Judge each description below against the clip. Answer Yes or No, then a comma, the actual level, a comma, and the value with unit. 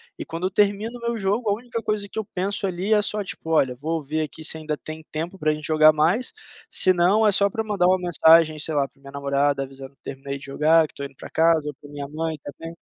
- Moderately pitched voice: Yes, medium, 160 Hz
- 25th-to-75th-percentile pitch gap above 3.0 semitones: Yes, average, 5.0 semitones